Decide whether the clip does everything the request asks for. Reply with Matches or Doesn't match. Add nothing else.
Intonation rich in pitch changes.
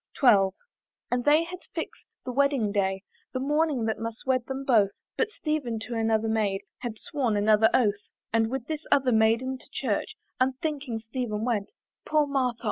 Doesn't match